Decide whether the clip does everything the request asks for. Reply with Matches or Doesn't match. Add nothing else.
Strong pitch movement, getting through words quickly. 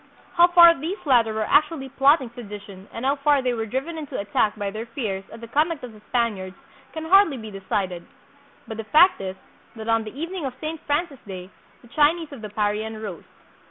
Matches